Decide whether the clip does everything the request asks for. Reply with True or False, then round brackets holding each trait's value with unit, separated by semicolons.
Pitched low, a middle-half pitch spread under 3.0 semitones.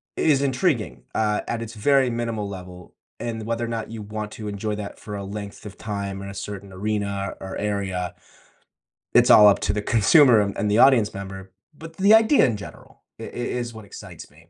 True (105 Hz; 2.6 semitones)